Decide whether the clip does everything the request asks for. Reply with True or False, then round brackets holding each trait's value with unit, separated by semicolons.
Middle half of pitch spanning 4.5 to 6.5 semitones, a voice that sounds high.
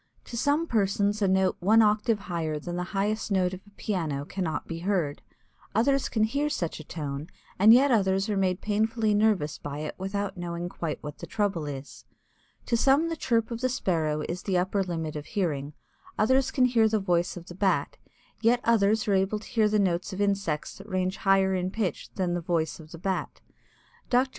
False (4.1 semitones; 195 Hz)